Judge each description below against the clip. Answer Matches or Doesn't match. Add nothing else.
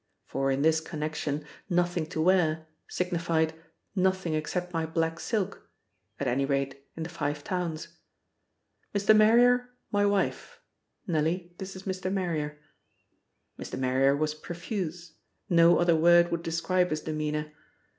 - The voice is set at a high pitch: Doesn't match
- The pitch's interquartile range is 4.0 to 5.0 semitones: Doesn't match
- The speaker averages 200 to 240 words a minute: Doesn't match